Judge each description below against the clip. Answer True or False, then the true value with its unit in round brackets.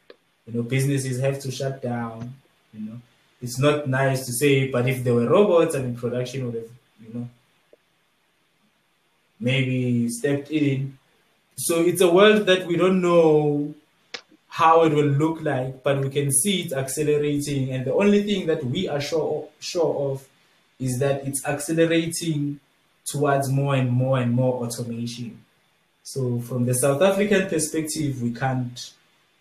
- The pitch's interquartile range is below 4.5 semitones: True (3.8 semitones)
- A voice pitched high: False (135 Hz)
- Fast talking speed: False (160 wpm)